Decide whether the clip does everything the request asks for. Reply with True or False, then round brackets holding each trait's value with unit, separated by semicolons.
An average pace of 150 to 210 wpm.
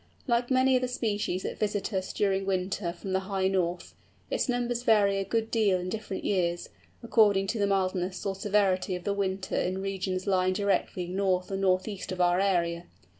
True (190 wpm)